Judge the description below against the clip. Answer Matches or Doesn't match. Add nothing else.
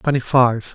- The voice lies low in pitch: Matches